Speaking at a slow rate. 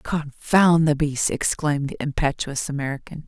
Yes: slow, 130 wpm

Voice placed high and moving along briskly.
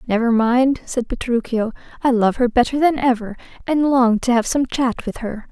No: high, 245 Hz; average, 195 wpm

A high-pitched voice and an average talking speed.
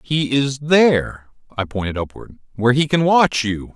No: low, 130 Hz; average, 160 wpm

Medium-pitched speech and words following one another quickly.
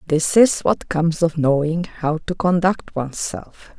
No: medium, 165 Hz; average, 160 wpm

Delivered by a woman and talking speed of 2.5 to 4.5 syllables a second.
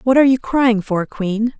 No: female; 4.8 syllables/s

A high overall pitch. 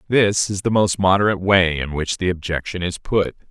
No: very low, 95 Hz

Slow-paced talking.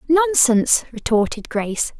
Yes: slow, 90 wpm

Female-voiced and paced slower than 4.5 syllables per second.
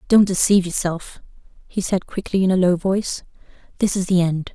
No: female; 5.7 syllables/s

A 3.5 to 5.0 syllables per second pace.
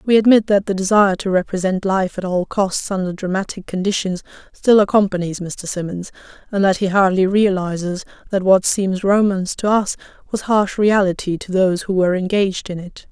No: 5.5 syllables/s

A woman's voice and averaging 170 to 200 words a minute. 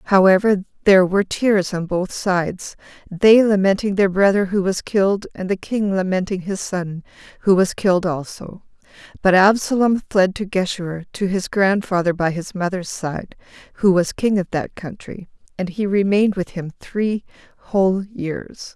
No: female; average, 160 wpm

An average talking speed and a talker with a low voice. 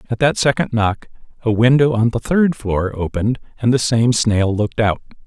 Yes: average, 195 wpm; low, 115 Hz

